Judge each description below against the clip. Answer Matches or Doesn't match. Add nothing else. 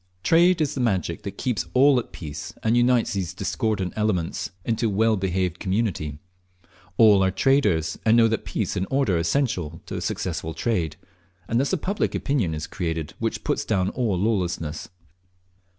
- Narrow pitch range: Doesn't match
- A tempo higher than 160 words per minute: Matches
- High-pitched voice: Doesn't match